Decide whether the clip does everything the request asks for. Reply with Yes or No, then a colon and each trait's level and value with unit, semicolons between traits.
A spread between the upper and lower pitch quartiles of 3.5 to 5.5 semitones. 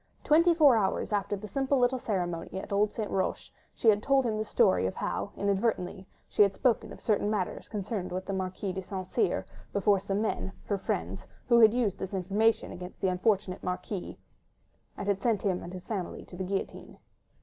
No: average, 2.9 semitones